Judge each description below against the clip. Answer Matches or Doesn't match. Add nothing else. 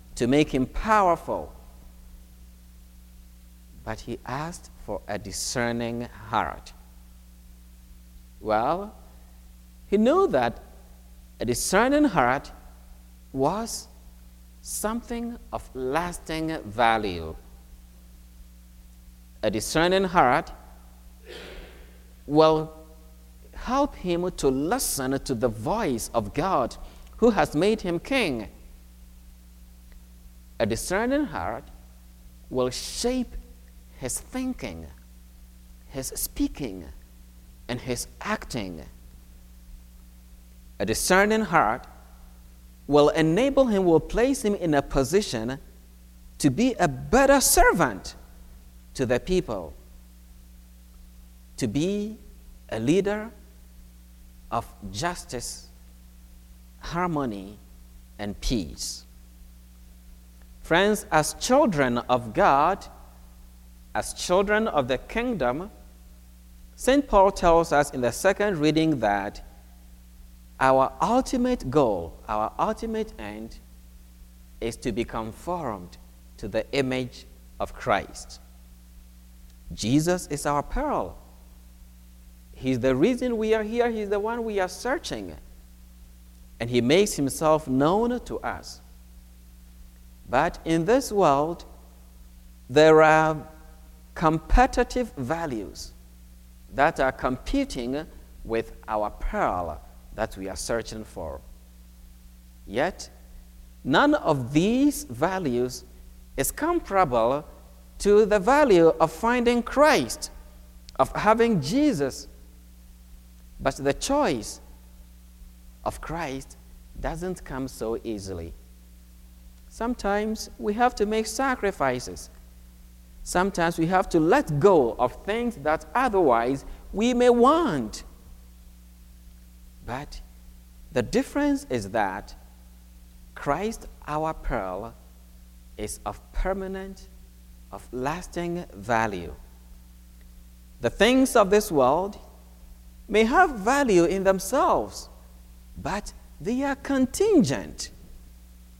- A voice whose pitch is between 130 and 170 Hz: Doesn't match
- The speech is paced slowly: Matches